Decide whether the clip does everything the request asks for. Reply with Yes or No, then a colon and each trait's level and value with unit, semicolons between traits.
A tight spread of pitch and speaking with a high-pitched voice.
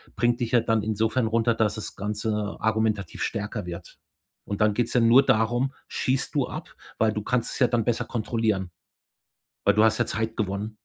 No: narrow, 1.9 semitones; low, 110 Hz